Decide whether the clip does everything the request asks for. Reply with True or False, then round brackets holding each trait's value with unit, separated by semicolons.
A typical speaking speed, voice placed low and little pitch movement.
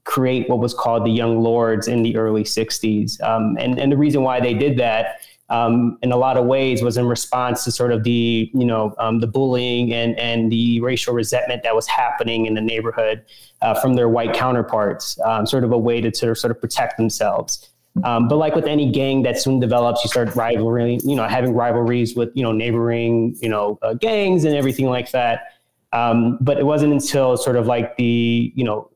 False (215 wpm; 120 Hz; 1.7 semitones)